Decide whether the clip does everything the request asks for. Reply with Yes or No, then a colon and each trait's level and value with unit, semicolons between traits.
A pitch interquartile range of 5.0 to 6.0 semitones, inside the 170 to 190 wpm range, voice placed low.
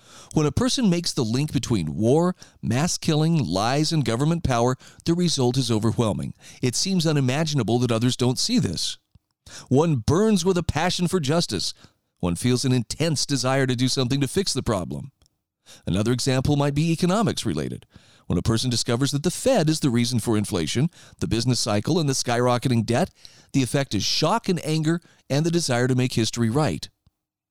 Yes: average, 5.3 semitones; average, 180 wpm; low, 130 Hz